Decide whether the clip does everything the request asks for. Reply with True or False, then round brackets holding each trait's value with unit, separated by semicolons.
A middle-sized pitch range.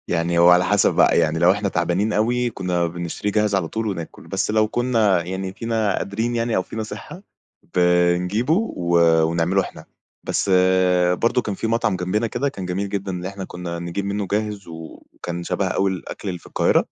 True (3.5 semitones)